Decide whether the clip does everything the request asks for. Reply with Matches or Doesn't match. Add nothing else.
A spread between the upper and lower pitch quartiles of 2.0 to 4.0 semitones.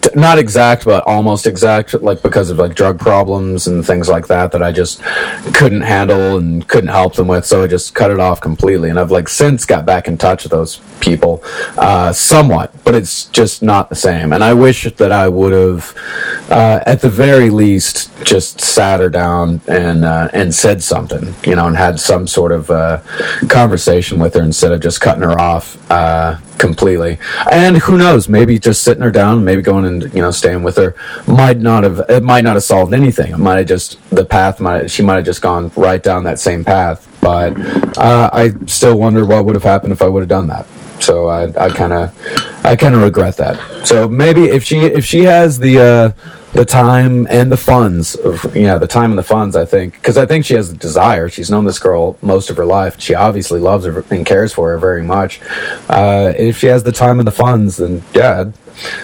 Doesn't match